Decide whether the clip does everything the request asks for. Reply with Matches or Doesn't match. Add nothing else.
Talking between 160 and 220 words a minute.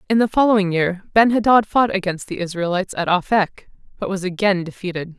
Matches